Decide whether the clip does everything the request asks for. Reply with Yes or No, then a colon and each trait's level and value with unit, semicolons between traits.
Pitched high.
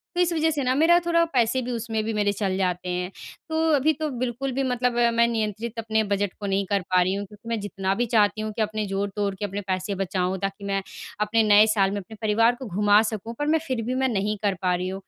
Yes: high, 215 Hz